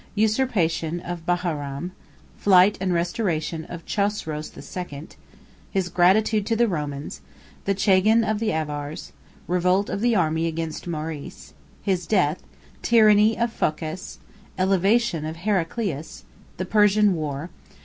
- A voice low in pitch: No, medium, 180 Hz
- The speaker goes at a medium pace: No, slow, 95 wpm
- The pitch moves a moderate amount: Yes, average, 4.5 semitones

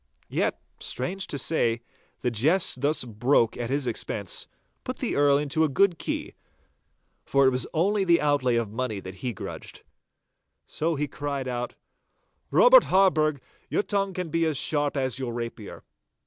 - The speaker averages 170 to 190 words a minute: No, average, 160 wpm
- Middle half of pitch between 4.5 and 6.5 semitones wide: Yes, average, 4.8 semitones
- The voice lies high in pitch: No, medium, 140 Hz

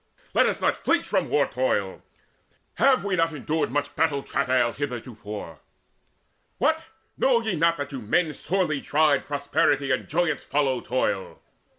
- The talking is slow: No, average, 150 wpm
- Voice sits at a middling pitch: Yes, medium, 145 Hz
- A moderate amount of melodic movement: Yes, average, 4.4 semitones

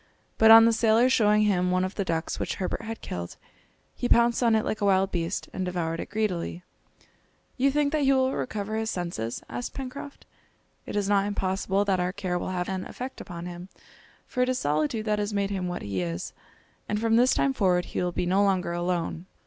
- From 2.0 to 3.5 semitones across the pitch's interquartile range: No, average, 4.0 semitones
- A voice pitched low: No, high, 200 Hz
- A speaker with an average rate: No, fast, 220 wpm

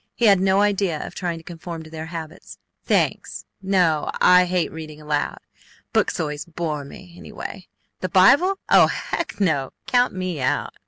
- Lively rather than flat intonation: No, average, 3.2 semitones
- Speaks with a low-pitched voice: No, medium, 175 Hz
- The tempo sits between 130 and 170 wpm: Yes, average, 165 wpm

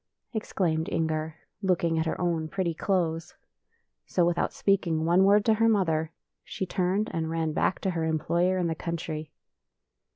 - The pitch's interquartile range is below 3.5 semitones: Yes, average, 2.8 semitones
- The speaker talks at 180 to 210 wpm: No, average, 165 wpm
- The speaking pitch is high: No, medium, 170 Hz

